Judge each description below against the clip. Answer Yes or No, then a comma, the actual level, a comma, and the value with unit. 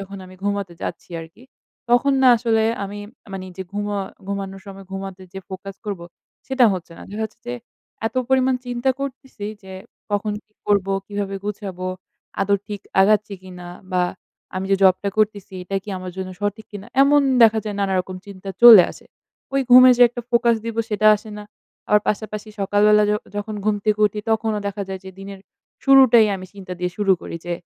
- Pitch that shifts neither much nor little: No, narrow, 2.3 semitones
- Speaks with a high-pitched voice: Yes, high, 205 Hz